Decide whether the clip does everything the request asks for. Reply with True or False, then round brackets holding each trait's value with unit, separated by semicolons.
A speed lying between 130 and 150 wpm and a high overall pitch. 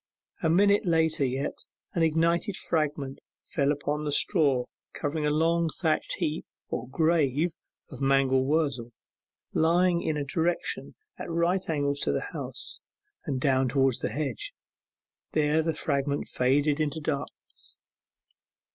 False (140 wpm; 150 Hz)